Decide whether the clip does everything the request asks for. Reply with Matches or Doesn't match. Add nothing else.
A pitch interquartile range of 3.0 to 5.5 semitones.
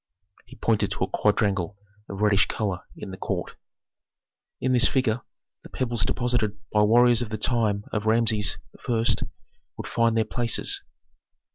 Doesn't match